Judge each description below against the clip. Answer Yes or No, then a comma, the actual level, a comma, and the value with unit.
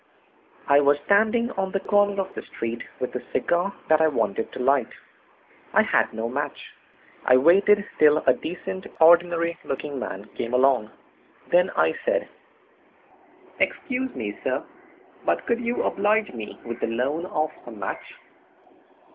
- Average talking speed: Yes, average, 150 wpm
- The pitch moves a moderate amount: No, wide, 7.7 semitones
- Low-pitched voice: No, medium, 155 Hz